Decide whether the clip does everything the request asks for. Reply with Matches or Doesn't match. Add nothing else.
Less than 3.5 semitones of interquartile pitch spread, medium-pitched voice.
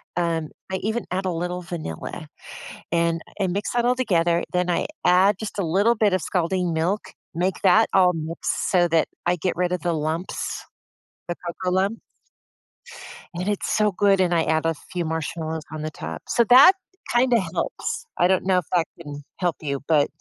Matches